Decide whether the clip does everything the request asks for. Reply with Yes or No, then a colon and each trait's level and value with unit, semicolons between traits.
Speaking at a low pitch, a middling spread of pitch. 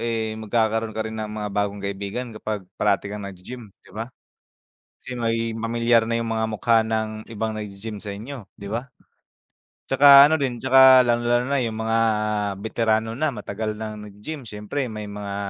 No: low, 110 Hz; narrow, 2.1 semitones